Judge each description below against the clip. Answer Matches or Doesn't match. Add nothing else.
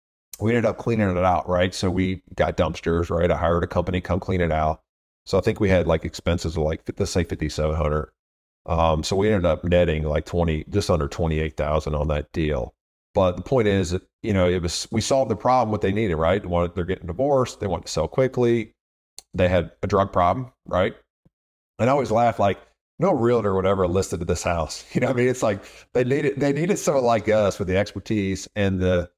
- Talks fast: Matches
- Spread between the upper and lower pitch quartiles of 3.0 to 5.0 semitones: Matches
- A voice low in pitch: Matches